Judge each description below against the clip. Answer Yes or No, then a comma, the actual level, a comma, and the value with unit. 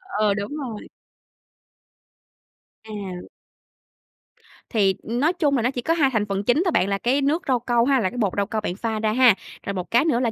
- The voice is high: Yes, high, 235 Hz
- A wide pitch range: No, average, 4.7 semitones